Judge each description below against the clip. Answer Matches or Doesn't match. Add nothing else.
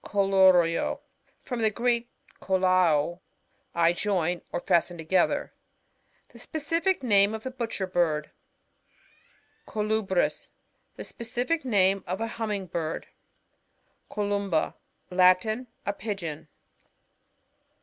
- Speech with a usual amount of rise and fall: Matches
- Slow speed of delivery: Matches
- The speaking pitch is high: Matches